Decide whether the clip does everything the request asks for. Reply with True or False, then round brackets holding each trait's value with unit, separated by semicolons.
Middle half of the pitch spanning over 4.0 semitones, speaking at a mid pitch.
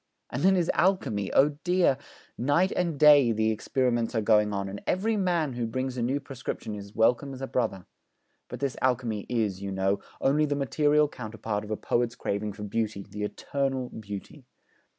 False (5.3 semitones; 125 Hz)